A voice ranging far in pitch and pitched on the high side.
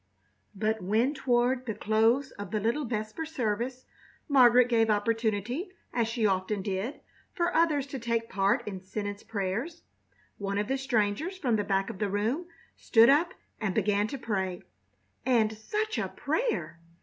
No: average, 4.2 semitones; high, 225 Hz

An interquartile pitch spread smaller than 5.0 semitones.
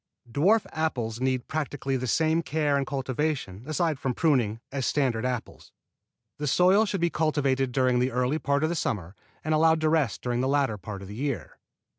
Yes: average, 4.0 semitones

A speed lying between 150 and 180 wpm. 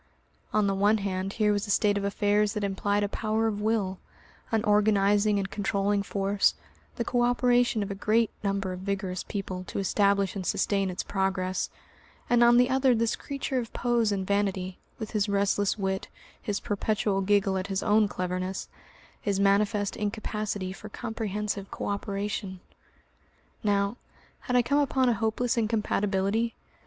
Yes: average, 165 wpm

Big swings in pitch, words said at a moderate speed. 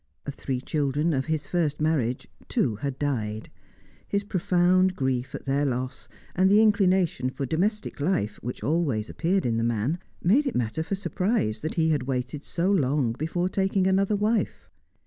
Yes: wide, 6.3 semitones; average, 170 wpm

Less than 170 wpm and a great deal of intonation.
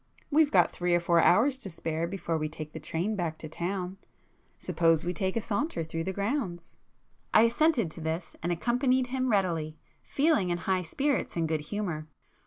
No: average, 185 wpm; wide, 5.8 semitones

